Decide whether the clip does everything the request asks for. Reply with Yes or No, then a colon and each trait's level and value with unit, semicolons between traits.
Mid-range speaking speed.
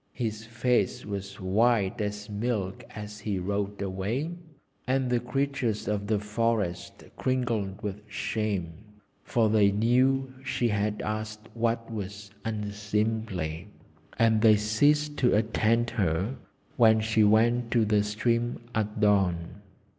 No: slow, 125 wpm